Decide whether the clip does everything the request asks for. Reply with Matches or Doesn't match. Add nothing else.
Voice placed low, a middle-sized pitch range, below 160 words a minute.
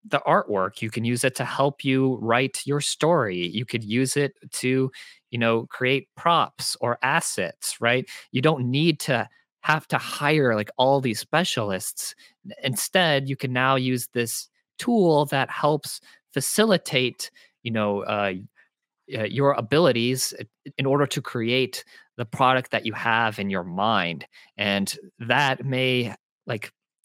Matches